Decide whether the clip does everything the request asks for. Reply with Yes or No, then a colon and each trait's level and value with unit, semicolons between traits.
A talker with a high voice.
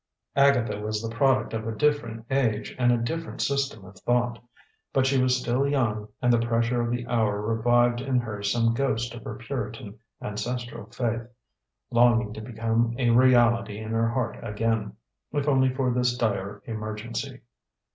No: low, 115 Hz